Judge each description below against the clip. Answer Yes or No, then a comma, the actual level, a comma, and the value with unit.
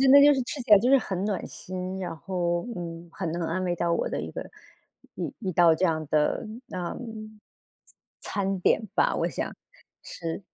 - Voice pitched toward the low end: No, medium, 185 Hz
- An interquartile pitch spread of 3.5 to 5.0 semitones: No, average, 2.8 semitones